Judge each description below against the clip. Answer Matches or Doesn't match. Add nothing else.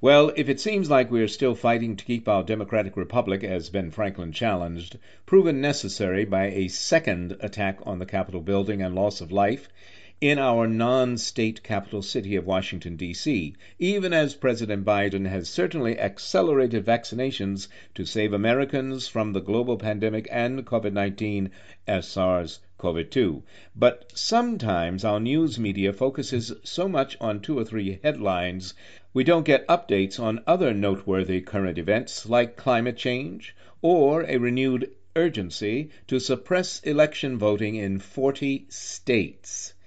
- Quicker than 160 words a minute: Doesn't match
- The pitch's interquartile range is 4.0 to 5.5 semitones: Matches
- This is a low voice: Matches